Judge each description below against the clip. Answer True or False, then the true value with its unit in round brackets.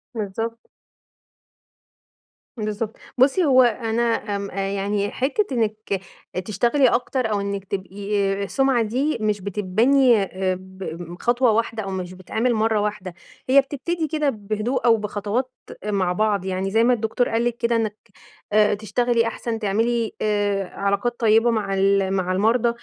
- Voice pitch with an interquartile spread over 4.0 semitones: False (3.2 semitones)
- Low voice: False (215 Hz)